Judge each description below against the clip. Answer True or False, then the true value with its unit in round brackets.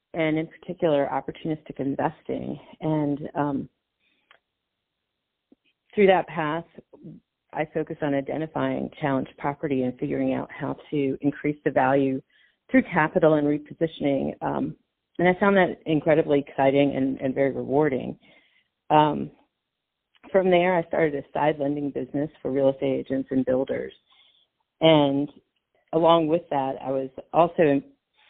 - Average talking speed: False (130 wpm)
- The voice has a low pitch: False (150 Hz)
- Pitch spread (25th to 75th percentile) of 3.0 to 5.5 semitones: False (2.6 semitones)